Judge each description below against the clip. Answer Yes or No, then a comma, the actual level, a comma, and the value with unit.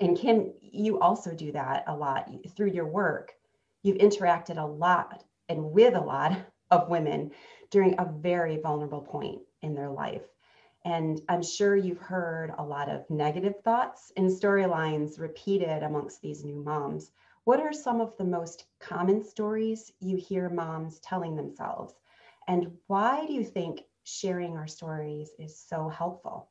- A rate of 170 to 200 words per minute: No, average, 160 wpm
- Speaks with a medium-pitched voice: Yes, medium, 175 Hz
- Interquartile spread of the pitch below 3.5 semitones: No, average, 4.0 semitones